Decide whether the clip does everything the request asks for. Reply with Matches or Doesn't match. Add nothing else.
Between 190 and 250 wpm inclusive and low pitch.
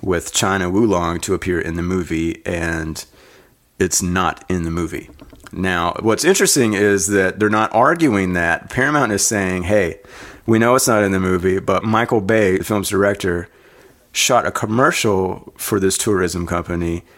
Doesn't match